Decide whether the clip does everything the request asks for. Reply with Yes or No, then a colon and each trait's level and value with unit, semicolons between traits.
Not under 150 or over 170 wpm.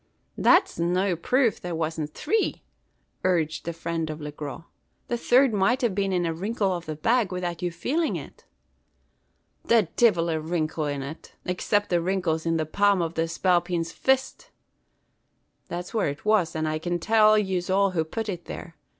No: average, 185 wpm